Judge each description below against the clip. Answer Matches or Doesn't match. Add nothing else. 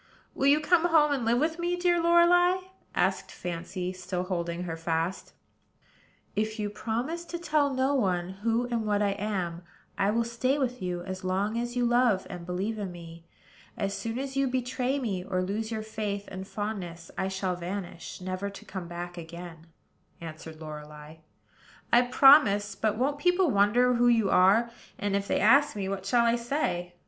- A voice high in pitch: Matches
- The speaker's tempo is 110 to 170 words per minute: Doesn't match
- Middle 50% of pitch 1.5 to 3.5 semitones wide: Doesn't match